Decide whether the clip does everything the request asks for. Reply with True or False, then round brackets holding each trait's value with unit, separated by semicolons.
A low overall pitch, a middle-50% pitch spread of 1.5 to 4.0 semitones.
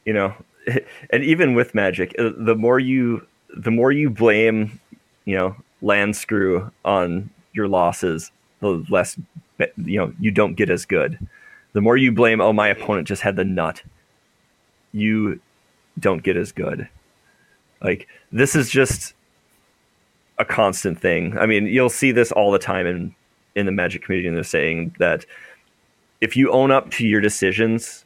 True (110 Hz; 3.5 semitones)